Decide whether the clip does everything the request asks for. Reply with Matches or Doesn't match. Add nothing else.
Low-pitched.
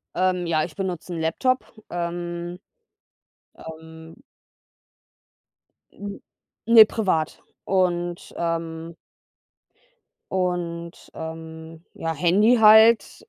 Doesn't match